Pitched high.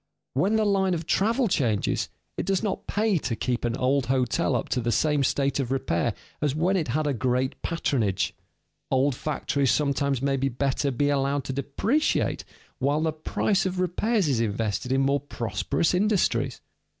No: medium, 140 Hz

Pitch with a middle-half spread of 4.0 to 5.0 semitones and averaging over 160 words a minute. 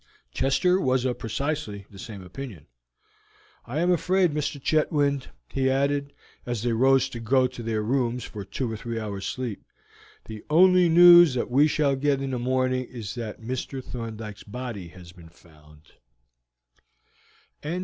No: average, 4.3 semitones; average, 155 wpm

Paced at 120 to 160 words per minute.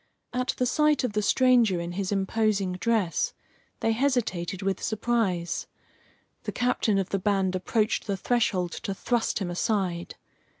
Yes: average, 145 wpm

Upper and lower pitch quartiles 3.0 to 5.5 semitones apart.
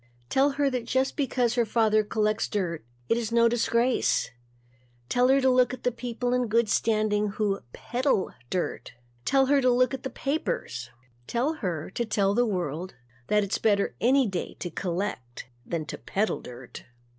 Yes: average, 4.2 semitones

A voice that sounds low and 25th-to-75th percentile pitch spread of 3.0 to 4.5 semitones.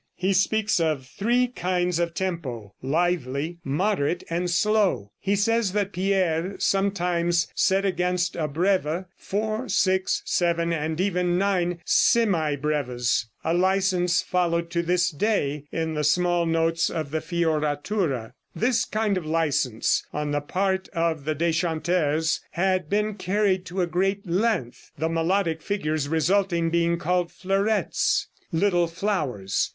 No: medium, 175 Hz; average, 3.3 semitones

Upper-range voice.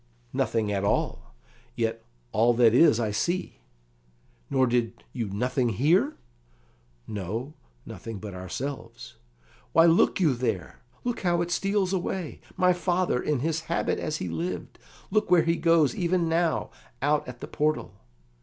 No: medium, 140 Hz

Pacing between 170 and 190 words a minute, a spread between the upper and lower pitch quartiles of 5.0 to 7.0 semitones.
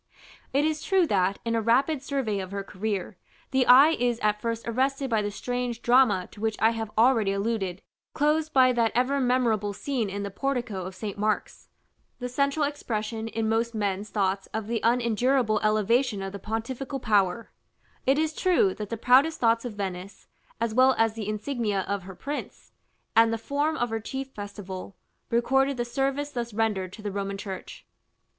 No: average, 185 wpm; average, 4.1 semitones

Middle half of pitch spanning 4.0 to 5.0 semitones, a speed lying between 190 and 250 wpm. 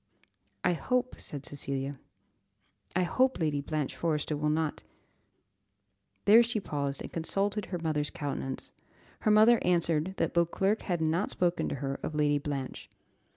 No: average, 4.5 semitones; average, 150 wpm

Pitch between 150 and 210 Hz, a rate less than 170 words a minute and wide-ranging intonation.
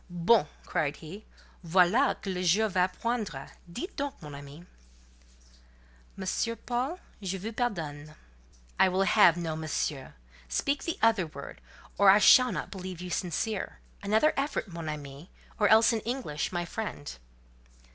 Yes: medium, 185 Hz; average, 140 wpm; wide, 5.7 semitones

